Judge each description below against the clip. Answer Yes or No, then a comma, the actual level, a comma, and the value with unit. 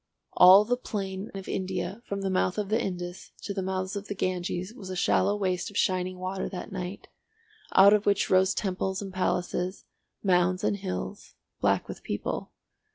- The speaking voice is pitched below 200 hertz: Yes, high, 190 Hz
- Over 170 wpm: Yes, average, 180 wpm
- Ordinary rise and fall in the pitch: No, narrow, 1.5 semitones